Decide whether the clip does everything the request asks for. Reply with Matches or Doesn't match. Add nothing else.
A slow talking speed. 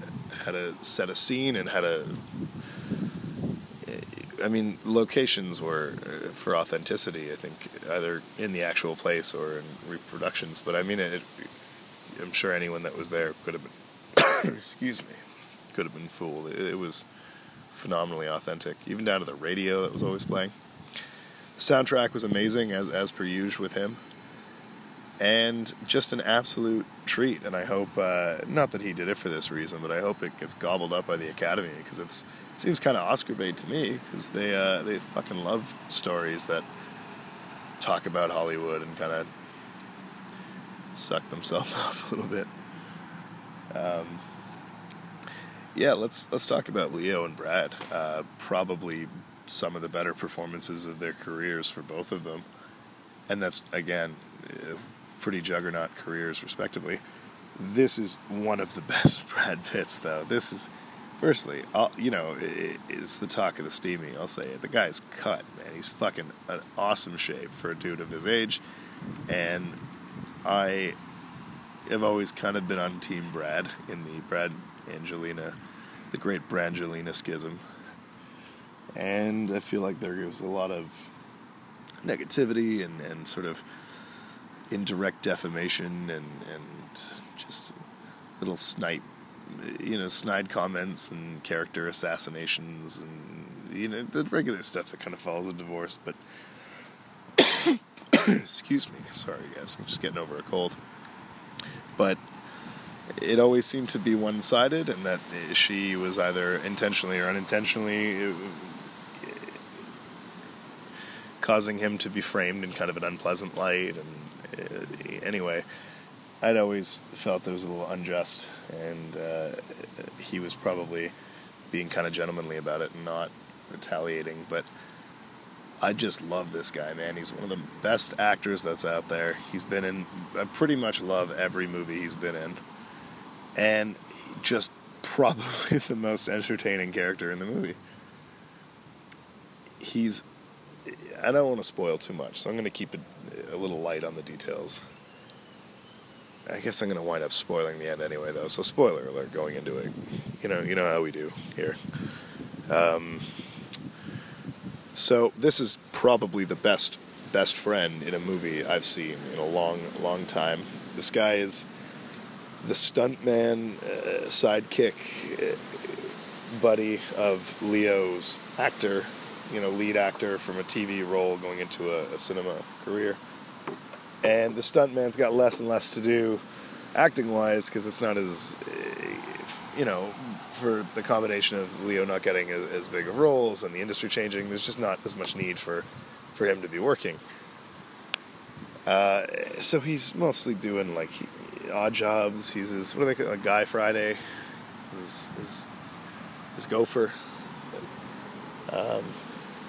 Doesn't match